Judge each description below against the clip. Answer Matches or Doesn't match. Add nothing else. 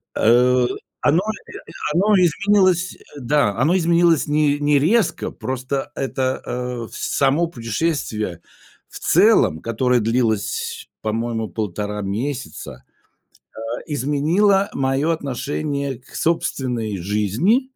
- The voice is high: Doesn't match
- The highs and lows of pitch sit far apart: Matches